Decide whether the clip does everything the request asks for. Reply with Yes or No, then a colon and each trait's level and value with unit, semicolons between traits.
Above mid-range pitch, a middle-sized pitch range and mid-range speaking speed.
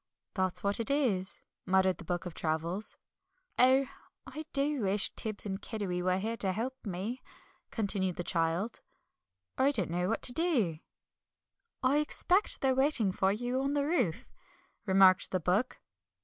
No: high, 205 Hz; wide, 5.9 semitones; average, 155 wpm